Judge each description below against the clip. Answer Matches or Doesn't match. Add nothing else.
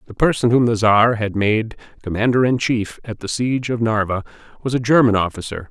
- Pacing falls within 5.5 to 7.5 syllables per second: Matches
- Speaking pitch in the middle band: Doesn't match